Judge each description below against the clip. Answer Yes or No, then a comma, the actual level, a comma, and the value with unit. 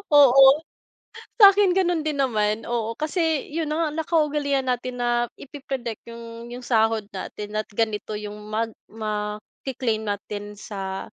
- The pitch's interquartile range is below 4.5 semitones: No, average, 5.1 semitones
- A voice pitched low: No, high, 240 Hz